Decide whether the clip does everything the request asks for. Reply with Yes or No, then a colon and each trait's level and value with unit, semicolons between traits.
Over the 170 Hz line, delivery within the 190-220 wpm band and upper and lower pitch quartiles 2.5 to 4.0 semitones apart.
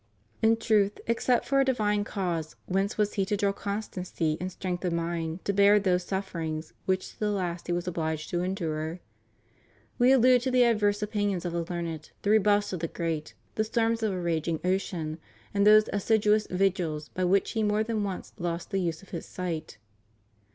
Yes: high, 190 Hz; average, 200 wpm; average, 3.5 semitones